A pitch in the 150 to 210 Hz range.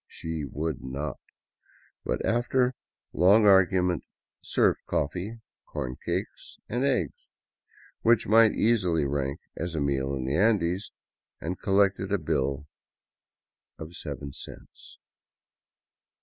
No: very low, 90 Hz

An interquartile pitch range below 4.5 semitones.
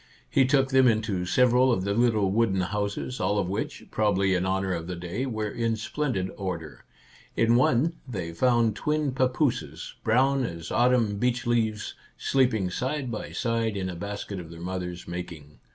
No: average, 5.1 semitones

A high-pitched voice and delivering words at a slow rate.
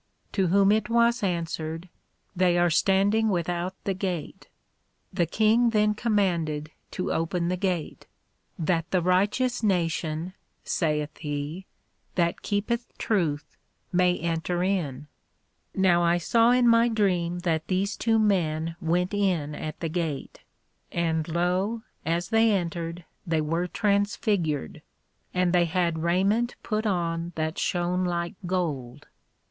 No: medium, 180 Hz; slow, 130 wpm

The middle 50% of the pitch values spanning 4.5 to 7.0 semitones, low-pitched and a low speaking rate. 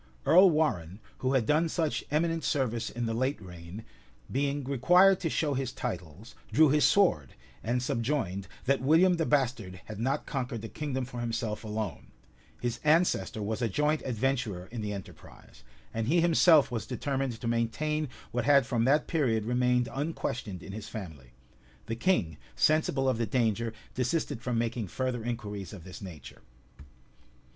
No: average, 5.0 semitones; low, 125 Hz; average, 165 wpm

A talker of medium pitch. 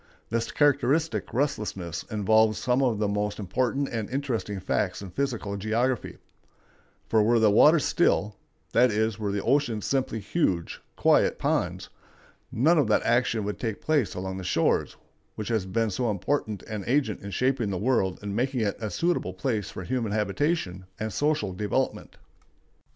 No: low, 110 Hz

